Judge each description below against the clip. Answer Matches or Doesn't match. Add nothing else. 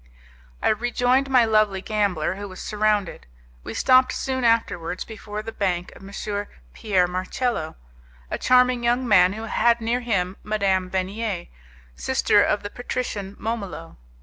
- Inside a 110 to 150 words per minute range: Matches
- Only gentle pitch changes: Doesn't match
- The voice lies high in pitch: Matches